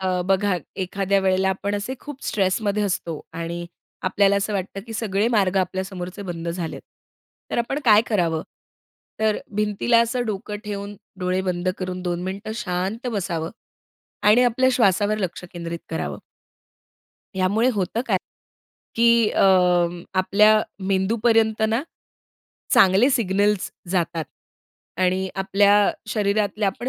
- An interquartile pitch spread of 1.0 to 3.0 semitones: Yes, narrow, 2.6 semitones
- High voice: Yes, high, 195 Hz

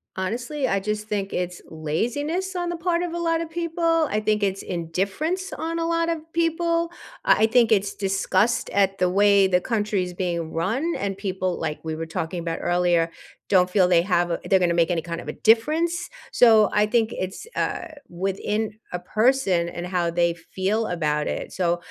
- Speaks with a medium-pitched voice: No, high, 200 Hz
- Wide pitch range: Yes, wide, 7.4 semitones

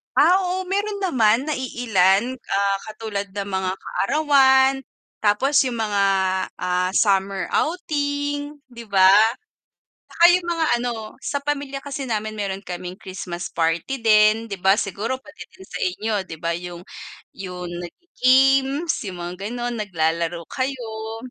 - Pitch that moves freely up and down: Yes, wide, 6.3 semitones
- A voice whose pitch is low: No, high, 220 Hz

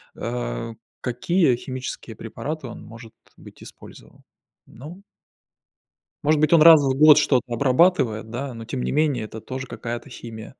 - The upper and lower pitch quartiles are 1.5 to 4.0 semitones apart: No, average, 4.8 semitones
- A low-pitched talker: Yes, low, 130 Hz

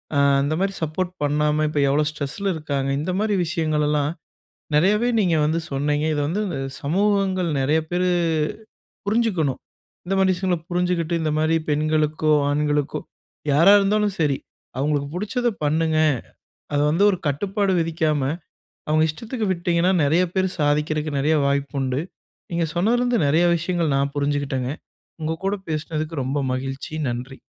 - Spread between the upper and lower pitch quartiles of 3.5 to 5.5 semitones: Yes, average, 3.8 semitones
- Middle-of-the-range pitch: Yes, medium, 155 Hz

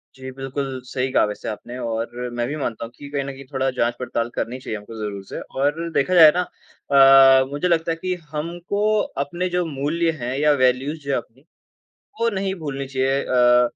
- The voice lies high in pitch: No, low, 135 Hz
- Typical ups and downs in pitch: Yes, average, 4.2 semitones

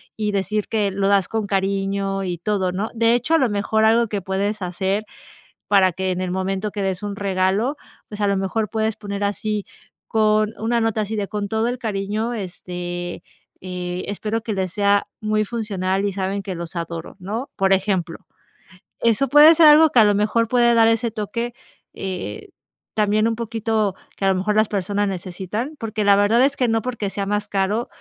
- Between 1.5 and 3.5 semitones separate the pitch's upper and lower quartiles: Yes, narrow, 2.5 semitones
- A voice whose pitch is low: No, high, 205 Hz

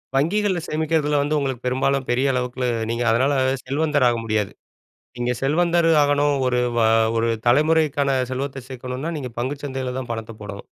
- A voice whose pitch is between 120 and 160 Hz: Yes, low, 135 Hz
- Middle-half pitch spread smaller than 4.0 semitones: Yes, average, 3.0 semitones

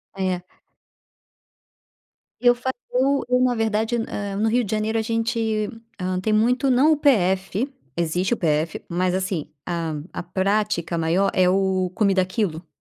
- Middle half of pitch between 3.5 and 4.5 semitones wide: Yes, average, 3.9 semitones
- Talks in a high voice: Yes, high, 200 Hz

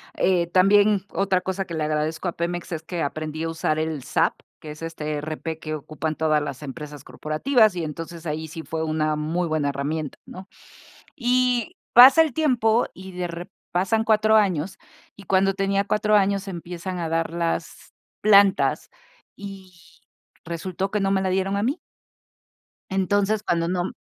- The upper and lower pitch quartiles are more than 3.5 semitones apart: Yes, average, 4.0 semitones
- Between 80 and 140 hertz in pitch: No, medium, 175 Hz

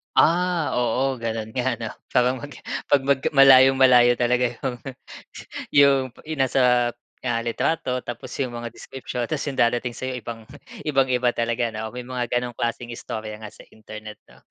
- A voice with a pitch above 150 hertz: No, low, 125 Hz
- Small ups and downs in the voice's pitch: Yes, narrow, 2.1 semitones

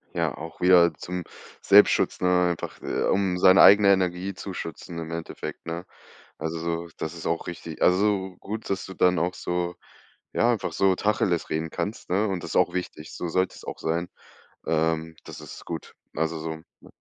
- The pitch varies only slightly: Yes, narrow, 2.3 semitones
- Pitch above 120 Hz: No, very low, 90 Hz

